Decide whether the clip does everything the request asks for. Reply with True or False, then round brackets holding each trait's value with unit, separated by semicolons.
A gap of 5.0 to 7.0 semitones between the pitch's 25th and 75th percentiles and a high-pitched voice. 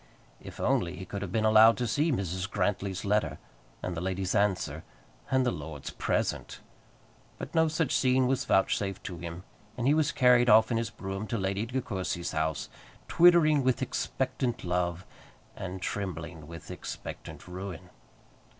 False (5.5 semitones; 100 Hz)